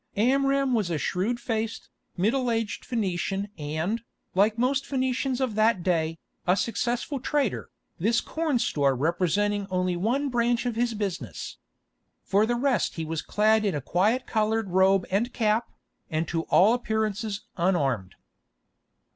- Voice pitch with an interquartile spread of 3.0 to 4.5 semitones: No, average, 5.0 semitones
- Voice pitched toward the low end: No, high, 215 Hz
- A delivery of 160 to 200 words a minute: No, average, 145 wpm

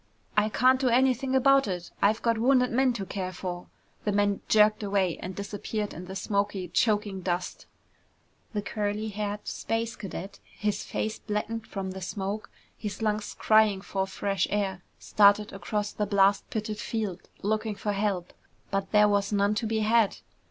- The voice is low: No, high, 205 Hz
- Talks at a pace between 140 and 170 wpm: Yes, average, 165 wpm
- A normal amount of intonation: No, narrow, 1.8 semitones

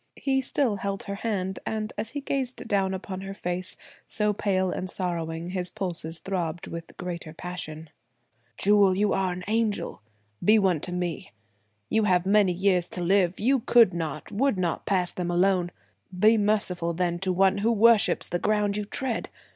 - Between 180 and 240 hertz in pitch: Yes, high, 190 Hz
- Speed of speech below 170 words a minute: No, average, 175 wpm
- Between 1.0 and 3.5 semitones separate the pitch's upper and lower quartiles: Yes, average, 2.8 semitones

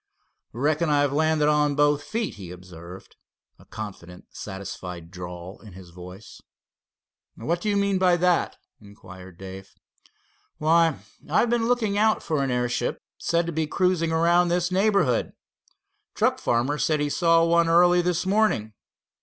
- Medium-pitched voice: Yes, medium, 150 Hz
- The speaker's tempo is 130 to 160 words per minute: Yes, average, 145 wpm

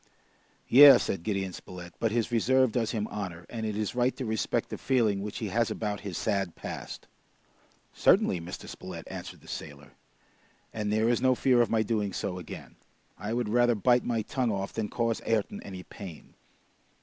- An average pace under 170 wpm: No, average, 185 wpm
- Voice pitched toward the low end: Yes, low, 110 Hz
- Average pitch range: Yes, average, 3.4 semitones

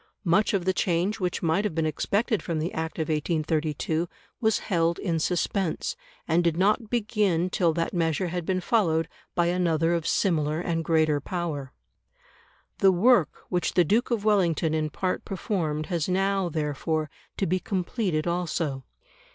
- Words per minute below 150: No, average, 160 wpm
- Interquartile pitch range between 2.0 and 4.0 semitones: Yes, average, 3.0 semitones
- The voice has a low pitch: No, medium, 170 Hz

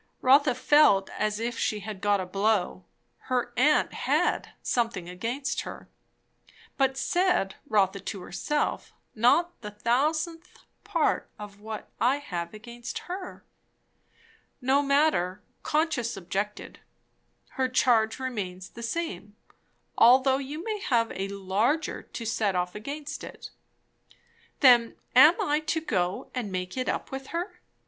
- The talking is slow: Yes, slow, 130 wpm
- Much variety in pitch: Yes, wide, 5.9 semitones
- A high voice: Yes, high, 235 Hz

